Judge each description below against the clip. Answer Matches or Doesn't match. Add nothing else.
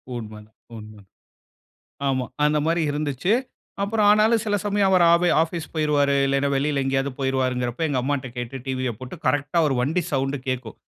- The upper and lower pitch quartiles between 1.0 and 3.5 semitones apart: Doesn't match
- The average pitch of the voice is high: Doesn't match